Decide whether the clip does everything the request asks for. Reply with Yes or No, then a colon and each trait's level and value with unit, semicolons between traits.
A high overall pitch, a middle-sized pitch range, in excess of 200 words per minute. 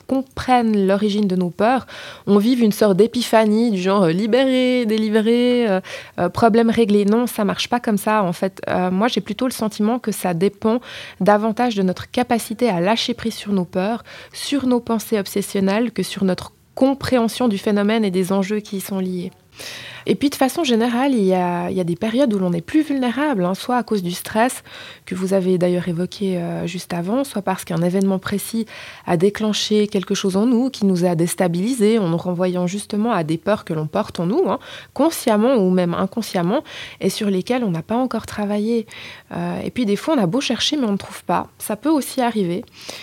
Yes: high, 210 Hz; average, 4.1 semitones; average, 210 wpm